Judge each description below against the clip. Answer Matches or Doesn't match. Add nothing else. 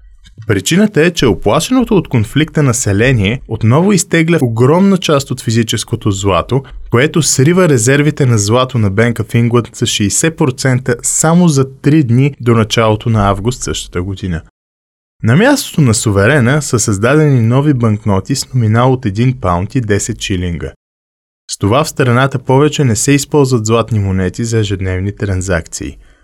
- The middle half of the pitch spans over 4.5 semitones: Matches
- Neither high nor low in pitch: Doesn't match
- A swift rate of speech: Doesn't match